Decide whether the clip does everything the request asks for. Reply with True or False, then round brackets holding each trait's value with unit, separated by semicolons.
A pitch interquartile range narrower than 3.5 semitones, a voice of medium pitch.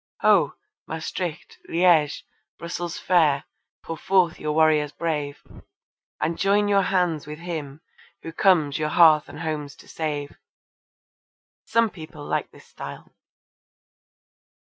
True (2.6 semitones; 160 Hz)